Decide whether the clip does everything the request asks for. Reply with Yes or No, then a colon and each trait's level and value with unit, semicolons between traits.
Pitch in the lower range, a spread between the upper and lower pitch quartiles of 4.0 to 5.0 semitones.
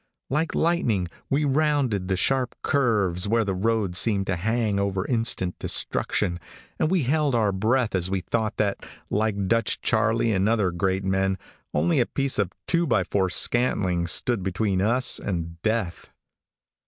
Yes: low, 105 Hz; average, 4.3 semitones